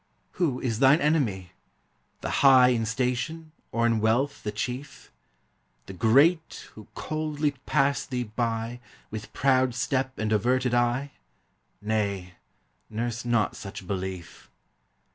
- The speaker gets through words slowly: Yes, slow, 125 wpm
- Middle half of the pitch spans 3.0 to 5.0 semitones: Yes, average, 3.9 semitones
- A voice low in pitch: Yes, low, 120 Hz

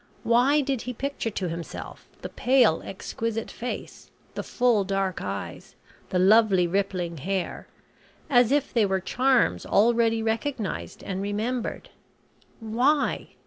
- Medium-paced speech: No, slow, 125 wpm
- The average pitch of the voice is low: No, high, 225 Hz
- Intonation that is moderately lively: Yes, average, 4.3 semitones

